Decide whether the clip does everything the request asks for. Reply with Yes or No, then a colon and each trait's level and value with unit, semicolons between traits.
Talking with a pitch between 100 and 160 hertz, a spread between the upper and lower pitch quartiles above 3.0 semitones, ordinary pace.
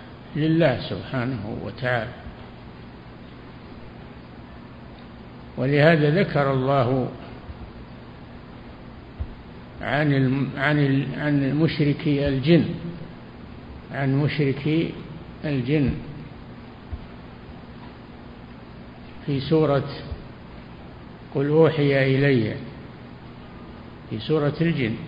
No: low, 135 Hz; average, 4.2 semitones; slow, 55 wpm